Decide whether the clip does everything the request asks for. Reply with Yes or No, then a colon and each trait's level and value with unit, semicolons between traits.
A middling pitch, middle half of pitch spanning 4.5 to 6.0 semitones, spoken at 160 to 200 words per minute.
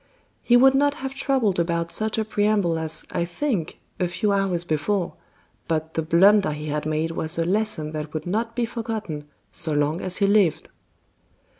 Yes: medium, 180 Hz; average, 5.3 semitones; average, 180 wpm